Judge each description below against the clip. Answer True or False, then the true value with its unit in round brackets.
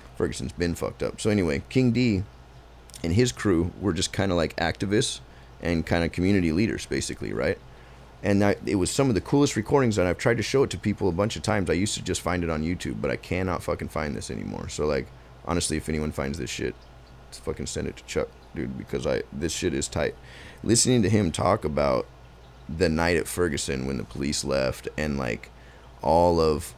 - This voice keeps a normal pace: False (220 wpm)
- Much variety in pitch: True (6.9 semitones)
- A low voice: True (85 Hz)